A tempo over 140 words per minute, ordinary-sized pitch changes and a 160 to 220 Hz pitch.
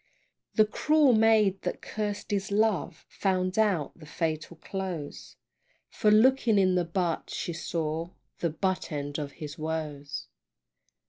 No: slow, 135 wpm; average, 4.9 semitones; medium, 185 Hz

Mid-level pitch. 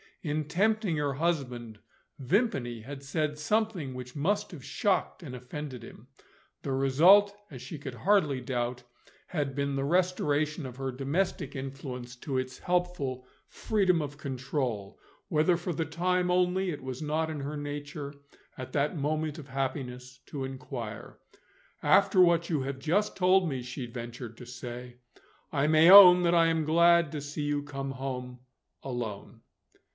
Yes: medium, 145 Hz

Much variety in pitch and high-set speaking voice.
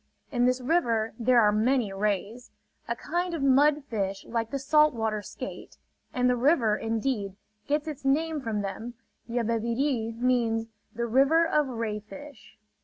No: average, 3.9 semitones; high, 240 Hz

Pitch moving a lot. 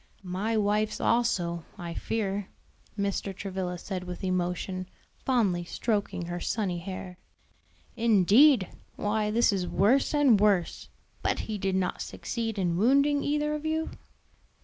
No: average, 4.1 semitones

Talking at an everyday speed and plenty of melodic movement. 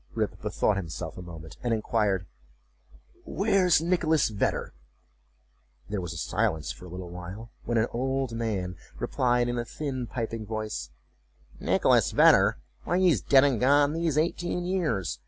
Yes: average, 150 wpm; wide, 8.0 semitones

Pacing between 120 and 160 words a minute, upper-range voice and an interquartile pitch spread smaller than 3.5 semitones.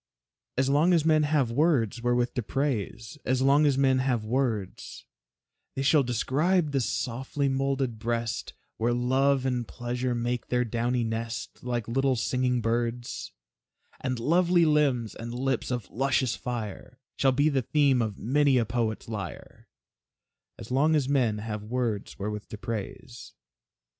No: average, 150 wpm; low, 125 Hz; average, 2.9 semitones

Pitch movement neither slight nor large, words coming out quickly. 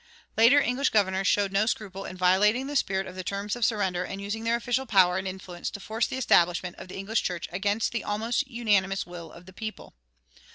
Yes: average, 3.4 semitones; fast, 215 wpm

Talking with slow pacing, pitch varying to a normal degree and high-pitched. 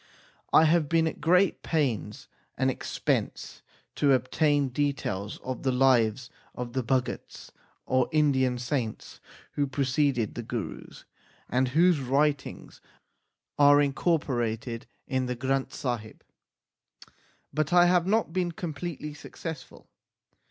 No: slow, 115 wpm; average, 3.6 semitones; low, 135 Hz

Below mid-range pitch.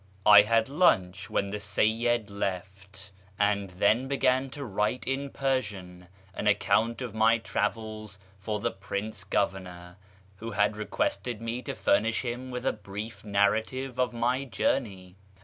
Yes: low, 105 Hz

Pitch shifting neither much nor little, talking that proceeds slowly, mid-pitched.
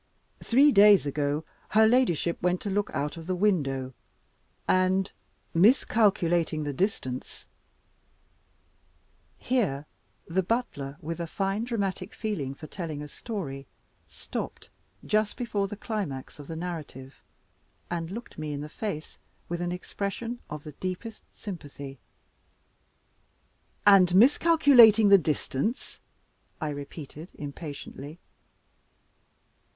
No: wide, 5.9 semitones; slow, 115 wpm; medium, 180 Hz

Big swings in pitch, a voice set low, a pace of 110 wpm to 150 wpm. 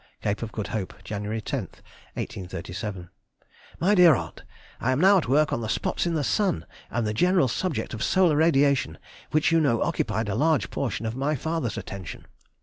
No: wide, 7.0 semitones; low, 130 Hz; average, 185 wpm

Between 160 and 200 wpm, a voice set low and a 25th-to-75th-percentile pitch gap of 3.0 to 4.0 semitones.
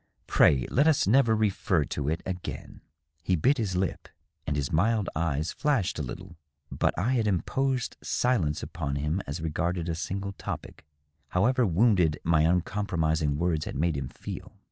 No: average, 165 wpm; very low, 90 Hz; wide, 5.4 semitones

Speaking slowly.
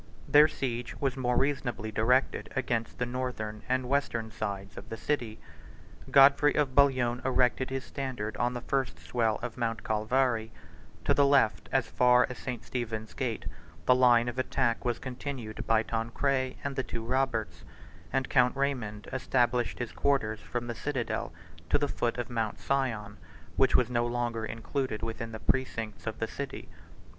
No: average, 165 wpm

